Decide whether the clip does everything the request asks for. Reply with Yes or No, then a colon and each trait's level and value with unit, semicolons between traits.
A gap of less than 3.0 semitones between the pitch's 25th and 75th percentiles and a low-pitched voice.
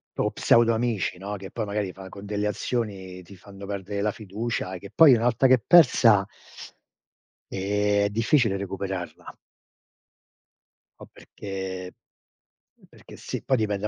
Yes: narrow, 2.6 semitones; low, 100 Hz